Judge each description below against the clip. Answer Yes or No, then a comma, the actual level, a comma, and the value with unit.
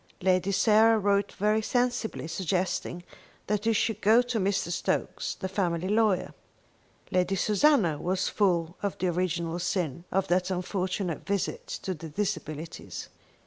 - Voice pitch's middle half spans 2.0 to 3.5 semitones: Yes, average, 3.1 semitones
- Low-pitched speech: No, high, 190 Hz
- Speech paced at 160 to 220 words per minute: No, average, 140 wpm